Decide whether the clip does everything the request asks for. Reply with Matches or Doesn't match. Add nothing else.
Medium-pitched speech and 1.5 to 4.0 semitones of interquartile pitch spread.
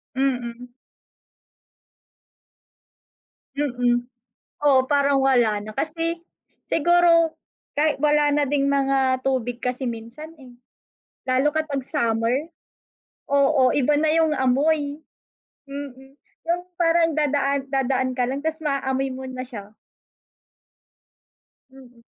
Doesn't match